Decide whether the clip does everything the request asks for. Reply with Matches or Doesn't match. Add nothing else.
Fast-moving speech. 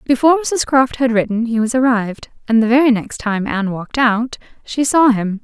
Matches